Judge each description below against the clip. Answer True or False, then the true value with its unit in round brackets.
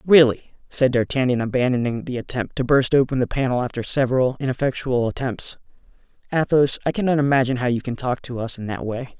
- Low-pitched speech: True (130 Hz)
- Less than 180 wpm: False (185 wpm)